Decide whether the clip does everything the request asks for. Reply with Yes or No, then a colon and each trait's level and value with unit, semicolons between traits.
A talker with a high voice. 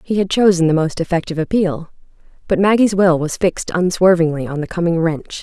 No: medium, 175 Hz